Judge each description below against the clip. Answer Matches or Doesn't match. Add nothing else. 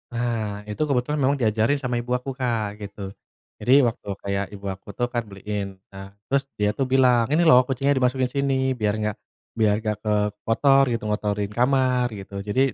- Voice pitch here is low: Matches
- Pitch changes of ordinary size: Matches